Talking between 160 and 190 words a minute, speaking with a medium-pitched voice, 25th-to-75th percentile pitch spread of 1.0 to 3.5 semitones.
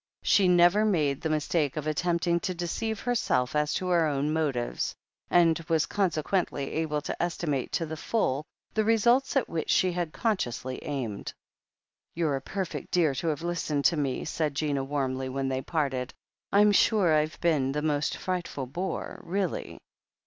No: average, 165 wpm; medium, 160 Hz; average, 4.0 semitones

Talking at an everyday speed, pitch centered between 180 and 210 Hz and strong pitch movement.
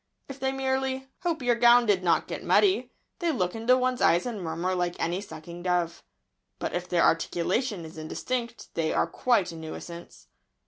Yes: average, 180 wpm; high, 190 Hz; wide, 6.9 semitones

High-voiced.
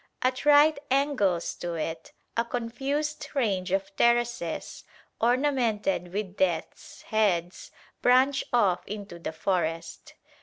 Yes: high, 215 Hz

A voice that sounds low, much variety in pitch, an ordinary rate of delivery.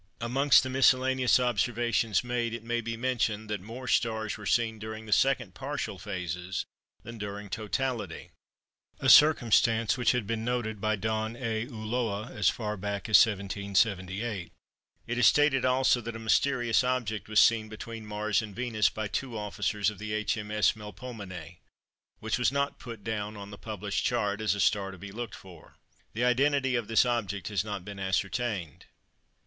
No: low, 110 Hz; average, 2.8 semitones; average, 165 wpm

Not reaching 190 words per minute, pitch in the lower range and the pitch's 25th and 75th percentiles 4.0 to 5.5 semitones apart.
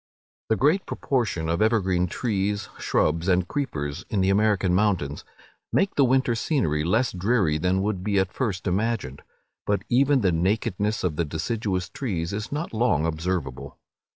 Yes: average, 155 wpm; low, 100 Hz; average, 4.8 semitones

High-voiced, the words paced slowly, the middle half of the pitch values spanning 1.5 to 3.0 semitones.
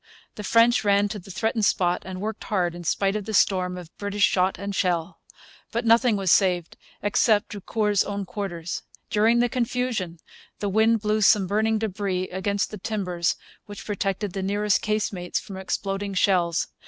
No: high, 200 Hz; average, 170 wpm; narrow, 2.5 semitones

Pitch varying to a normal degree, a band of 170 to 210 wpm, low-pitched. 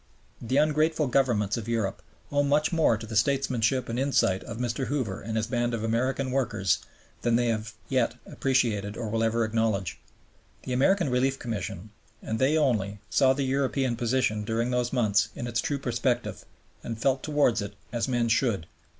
Yes: average, 3.2 semitones; average, 175 wpm; low, 120 Hz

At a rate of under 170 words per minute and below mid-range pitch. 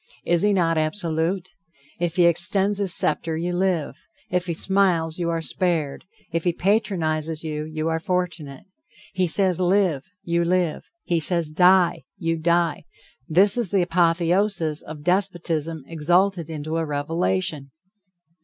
No: average, 145 wpm; medium, 170 Hz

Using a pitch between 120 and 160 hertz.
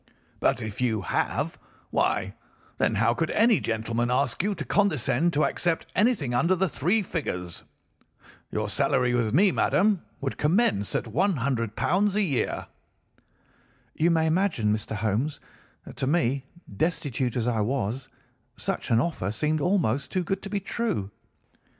Yes: medium, 140 Hz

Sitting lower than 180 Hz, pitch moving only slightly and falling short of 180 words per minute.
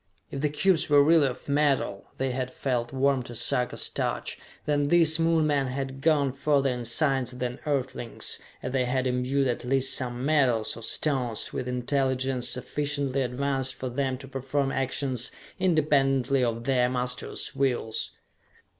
Yes: low, 135 Hz; narrow, 2.2 semitones; average, 155 wpm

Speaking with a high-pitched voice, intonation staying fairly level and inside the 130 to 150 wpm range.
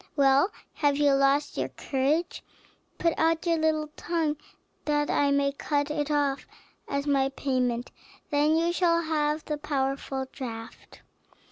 Yes: very high, 290 Hz; narrow, 2.3 semitones; average, 140 wpm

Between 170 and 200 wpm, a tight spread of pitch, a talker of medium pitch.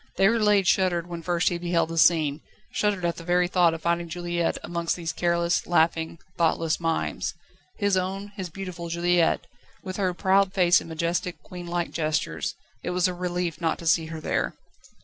Yes: average, 180 wpm; narrow, 1.5 semitones; medium, 175 Hz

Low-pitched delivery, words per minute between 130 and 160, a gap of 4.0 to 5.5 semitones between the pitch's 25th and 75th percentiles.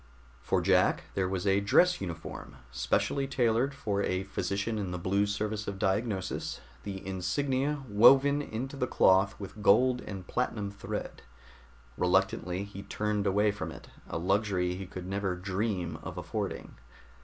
No: low, 100 Hz; average, 150 wpm; average, 2.9 semitones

